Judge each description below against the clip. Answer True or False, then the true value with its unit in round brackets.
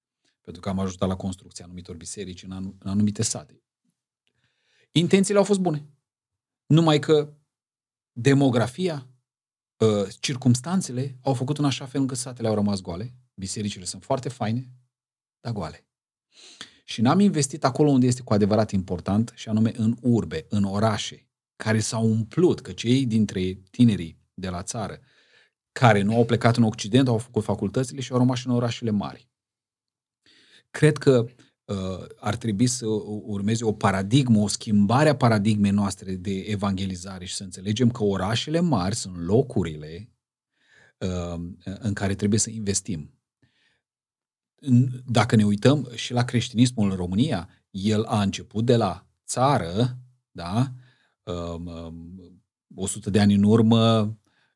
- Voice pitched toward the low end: True (110 Hz)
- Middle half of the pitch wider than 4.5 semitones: False (4.2 semitones)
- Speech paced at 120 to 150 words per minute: True (140 wpm)